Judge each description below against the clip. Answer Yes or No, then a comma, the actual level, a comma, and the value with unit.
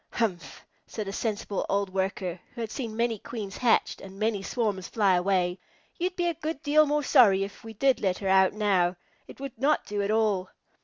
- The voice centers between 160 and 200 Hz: No, high, 210 Hz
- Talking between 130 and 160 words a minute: No, fast, 205 wpm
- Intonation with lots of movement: No, average, 3.8 semitones